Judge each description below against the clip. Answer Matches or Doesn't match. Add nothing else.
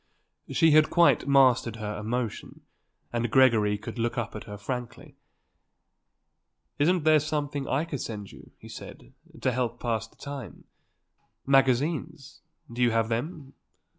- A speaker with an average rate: Matches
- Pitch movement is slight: Doesn't match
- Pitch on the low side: Matches